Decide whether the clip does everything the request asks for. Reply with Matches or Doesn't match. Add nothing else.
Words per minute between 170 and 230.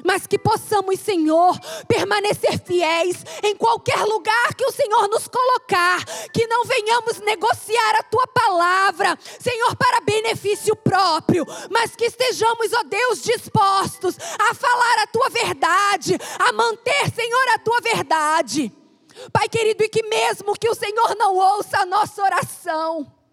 Doesn't match